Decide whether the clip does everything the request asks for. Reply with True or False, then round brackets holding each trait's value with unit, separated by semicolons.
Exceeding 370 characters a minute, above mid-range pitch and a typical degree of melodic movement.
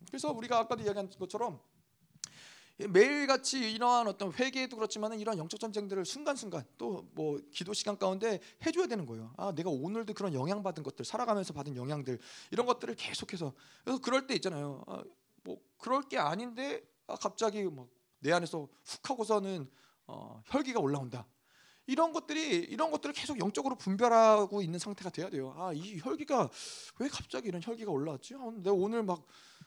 False (380 characters per minute; 205 Hz; 6.7 semitones)